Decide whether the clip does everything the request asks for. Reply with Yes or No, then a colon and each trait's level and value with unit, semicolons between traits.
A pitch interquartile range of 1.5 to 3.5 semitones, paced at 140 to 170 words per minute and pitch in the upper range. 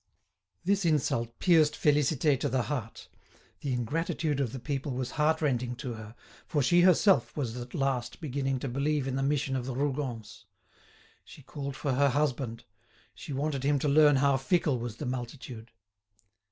No: average, 3.1 semitones; average, 165 wpm; low, 135 Hz